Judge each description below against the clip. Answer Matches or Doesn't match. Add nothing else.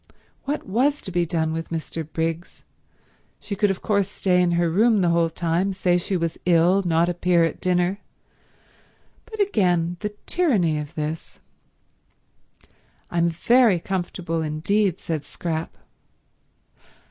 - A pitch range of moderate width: Matches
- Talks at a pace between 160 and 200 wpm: Doesn't match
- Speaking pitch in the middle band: Matches